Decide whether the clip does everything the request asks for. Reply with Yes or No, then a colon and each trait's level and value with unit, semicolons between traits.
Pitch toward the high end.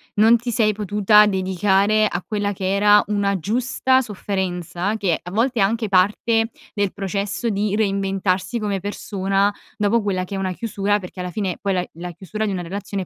Yes: high, 200 Hz